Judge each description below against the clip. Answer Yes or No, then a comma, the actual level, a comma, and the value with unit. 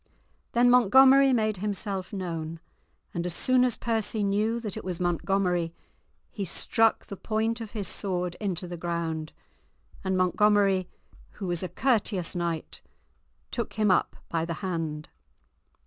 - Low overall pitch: No, high, 195 Hz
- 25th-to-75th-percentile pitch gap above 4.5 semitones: No, average, 3.9 semitones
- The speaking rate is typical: Yes, average, 145 wpm